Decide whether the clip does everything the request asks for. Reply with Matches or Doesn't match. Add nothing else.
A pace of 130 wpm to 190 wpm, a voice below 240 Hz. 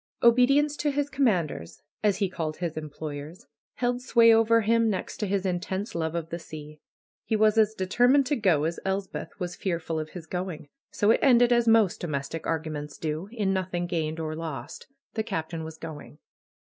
Matches